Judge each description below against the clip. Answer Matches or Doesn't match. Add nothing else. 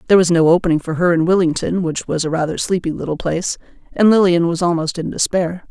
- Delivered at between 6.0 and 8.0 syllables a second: Matches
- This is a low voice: Doesn't match